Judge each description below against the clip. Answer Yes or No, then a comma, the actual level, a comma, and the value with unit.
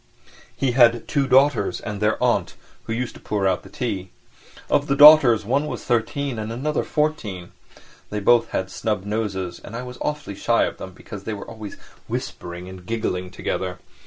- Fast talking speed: No, average, 185 wpm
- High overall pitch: No, low, 110 Hz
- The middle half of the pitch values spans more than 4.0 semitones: Yes, average, 4.8 semitones